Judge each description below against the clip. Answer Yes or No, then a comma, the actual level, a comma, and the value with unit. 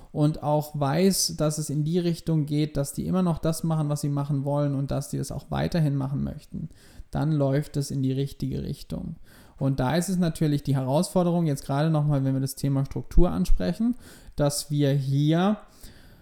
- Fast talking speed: Yes, fast, 205 wpm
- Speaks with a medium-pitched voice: Yes, medium, 150 Hz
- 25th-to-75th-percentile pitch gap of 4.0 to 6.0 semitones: No, average, 3.1 semitones